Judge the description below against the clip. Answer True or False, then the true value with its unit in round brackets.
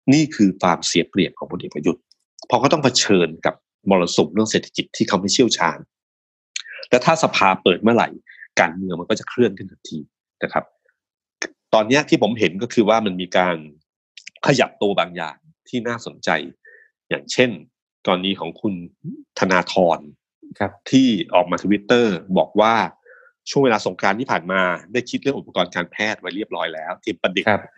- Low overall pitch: True (115 Hz)